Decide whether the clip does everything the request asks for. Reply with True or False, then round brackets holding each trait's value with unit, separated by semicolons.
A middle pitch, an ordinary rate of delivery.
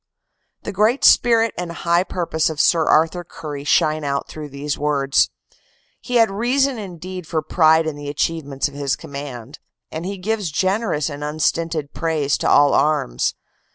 True (160 Hz; 165 wpm)